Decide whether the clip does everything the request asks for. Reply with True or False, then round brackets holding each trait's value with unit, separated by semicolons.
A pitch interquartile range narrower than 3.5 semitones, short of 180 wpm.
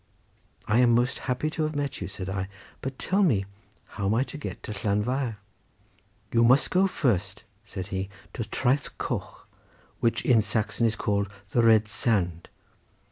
False (4.1 semitones; 170 wpm)